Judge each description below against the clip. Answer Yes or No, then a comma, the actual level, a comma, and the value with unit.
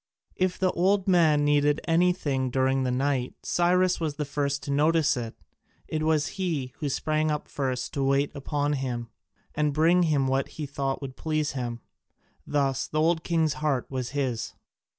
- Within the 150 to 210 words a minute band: Yes, average, 170 wpm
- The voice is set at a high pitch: No, medium, 145 Hz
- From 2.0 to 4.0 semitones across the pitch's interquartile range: Yes, average, 3.0 semitones